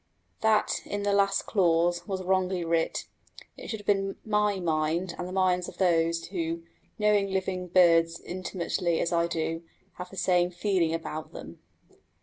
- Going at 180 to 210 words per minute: No, average, 160 wpm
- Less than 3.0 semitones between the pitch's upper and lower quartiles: Yes, narrow, 2.5 semitones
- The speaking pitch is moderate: Yes, medium, 180 Hz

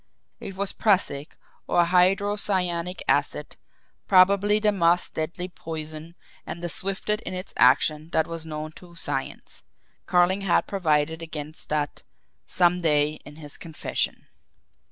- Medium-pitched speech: Yes, medium, 170 Hz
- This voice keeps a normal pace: No, slow, 130 wpm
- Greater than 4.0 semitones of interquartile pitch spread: No, average, 3.3 semitones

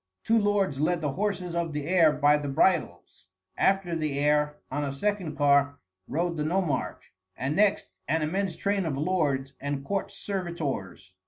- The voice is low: No, medium, 155 Hz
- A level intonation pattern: No, average, 4.6 semitones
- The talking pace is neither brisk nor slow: Yes, average, 165 wpm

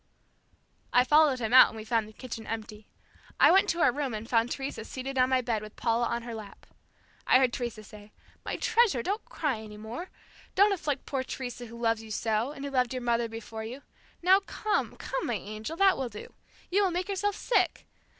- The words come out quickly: Yes, fast, 215 wpm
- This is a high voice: Yes, high, 245 Hz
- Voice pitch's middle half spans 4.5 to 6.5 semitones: Yes, average, 4.9 semitones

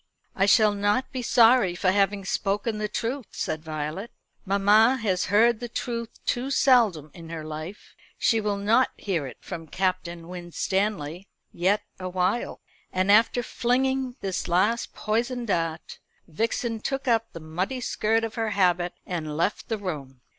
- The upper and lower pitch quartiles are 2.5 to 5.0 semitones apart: Yes, average, 4.6 semitones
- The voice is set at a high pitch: Yes, high, 200 Hz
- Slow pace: No, average, 155 wpm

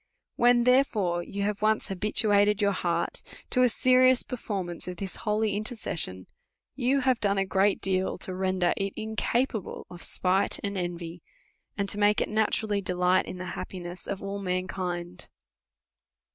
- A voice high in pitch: Yes, high, 200 Hz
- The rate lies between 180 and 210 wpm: No, average, 155 wpm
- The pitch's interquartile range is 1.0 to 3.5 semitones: Yes, average, 3.0 semitones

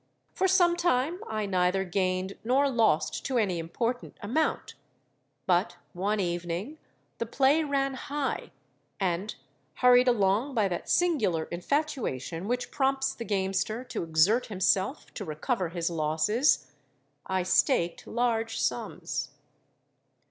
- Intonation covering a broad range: Yes, wide, 6.6 semitones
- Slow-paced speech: Yes, slow, 115 wpm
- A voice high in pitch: Yes, high, 210 Hz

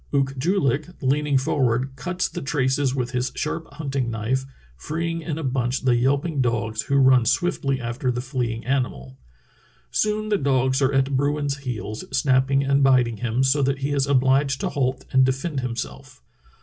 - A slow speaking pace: No, average, 175 wpm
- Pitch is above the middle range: No, low, 135 Hz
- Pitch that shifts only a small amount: Yes, narrow, 2.0 semitones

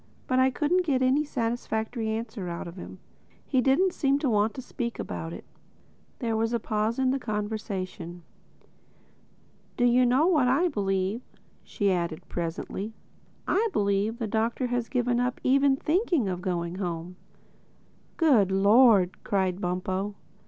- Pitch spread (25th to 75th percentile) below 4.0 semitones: No, average, 5.1 semitones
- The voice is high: Yes, high, 225 Hz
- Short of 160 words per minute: Yes, average, 150 wpm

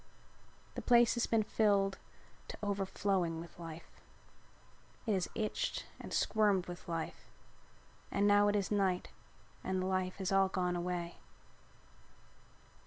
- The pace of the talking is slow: Yes, slow, 130 wpm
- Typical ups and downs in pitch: No, narrow, 2.3 semitones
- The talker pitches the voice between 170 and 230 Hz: Yes, high, 190 Hz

